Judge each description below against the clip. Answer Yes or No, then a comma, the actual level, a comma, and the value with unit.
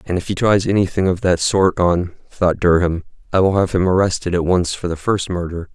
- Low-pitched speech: Yes, very low, 90 Hz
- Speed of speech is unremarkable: No, fast, 220 wpm